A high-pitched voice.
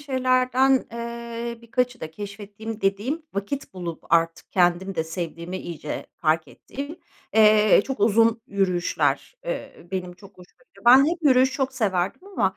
Yes: high, 215 Hz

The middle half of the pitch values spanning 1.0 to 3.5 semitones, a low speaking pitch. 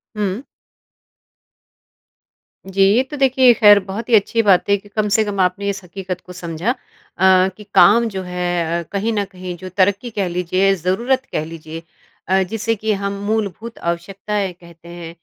No: average, 3.1 semitones; high, 195 Hz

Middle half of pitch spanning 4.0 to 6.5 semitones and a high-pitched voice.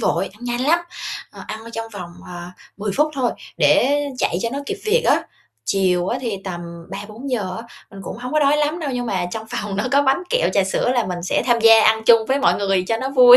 Yes: average, 5.3 semitones; high, 225 Hz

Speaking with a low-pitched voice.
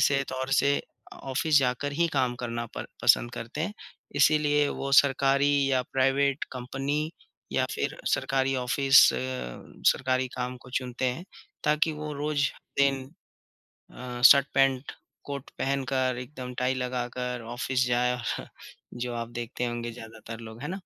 Yes: low, 130 Hz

